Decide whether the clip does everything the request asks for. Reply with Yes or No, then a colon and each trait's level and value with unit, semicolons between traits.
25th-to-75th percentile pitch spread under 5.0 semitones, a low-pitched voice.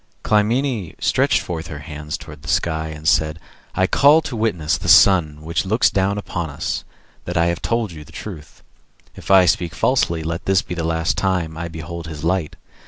Yes: average, 3.4 semitones; very low, 85 Hz